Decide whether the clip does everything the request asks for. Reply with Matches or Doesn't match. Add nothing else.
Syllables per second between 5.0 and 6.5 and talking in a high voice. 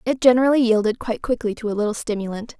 Doesn't match